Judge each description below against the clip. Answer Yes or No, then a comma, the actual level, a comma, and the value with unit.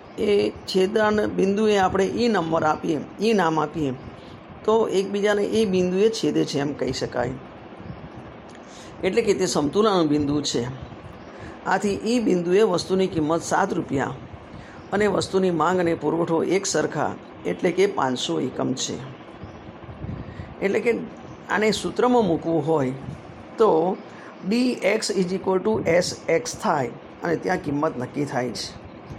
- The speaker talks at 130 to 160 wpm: Yes, average, 135 wpm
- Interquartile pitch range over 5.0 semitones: Yes, wide, 5.4 semitones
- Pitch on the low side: No, medium, 185 Hz